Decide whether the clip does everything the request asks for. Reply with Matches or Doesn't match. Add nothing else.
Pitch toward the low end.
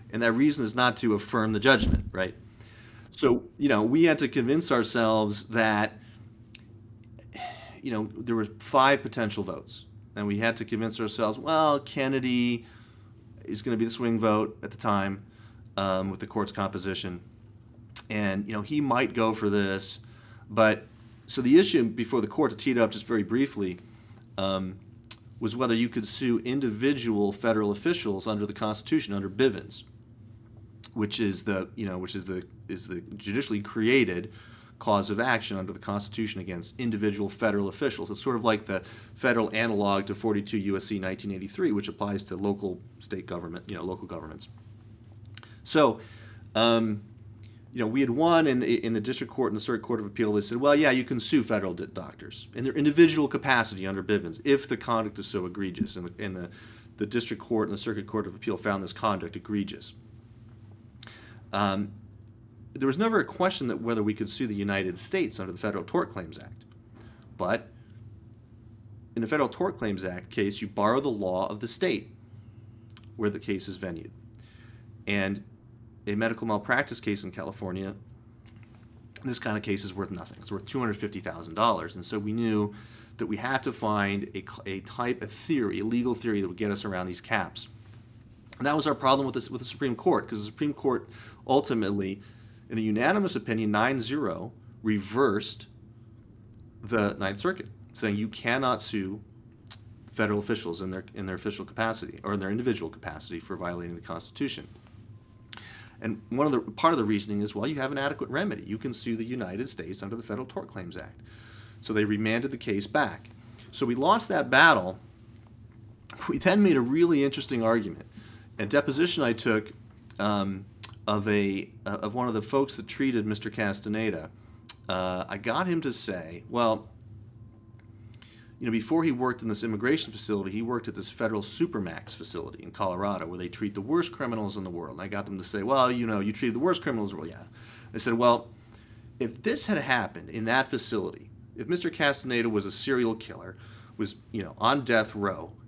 Matches